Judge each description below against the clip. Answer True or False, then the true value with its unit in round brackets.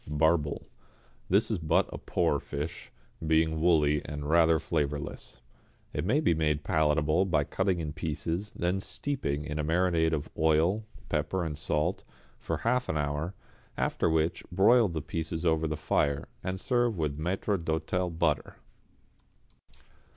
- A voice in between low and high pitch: False (80 Hz)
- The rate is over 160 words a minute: False (145 wpm)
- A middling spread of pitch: True (3.1 semitones)